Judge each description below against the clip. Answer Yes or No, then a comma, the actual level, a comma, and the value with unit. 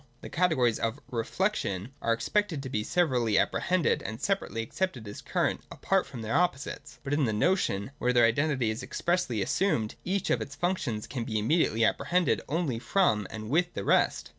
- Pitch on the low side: Yes, low, 130 Hz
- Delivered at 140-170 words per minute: No, average, 180 wpm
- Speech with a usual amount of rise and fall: No, wide, 7.8 semitones